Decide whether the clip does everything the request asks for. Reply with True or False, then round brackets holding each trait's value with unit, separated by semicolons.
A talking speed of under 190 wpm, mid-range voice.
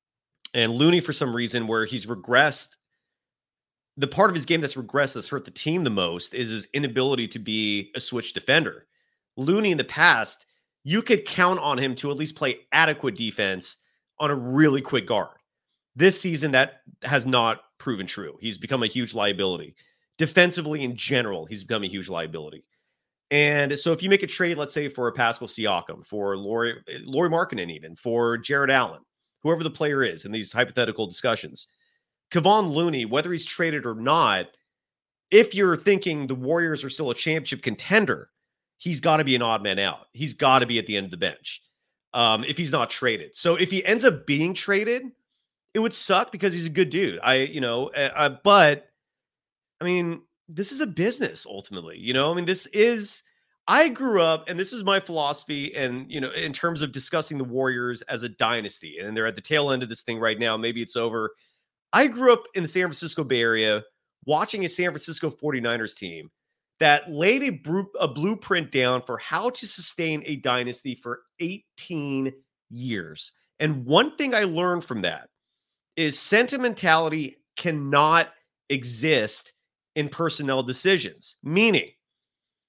True (180 wpm; 145 Hz)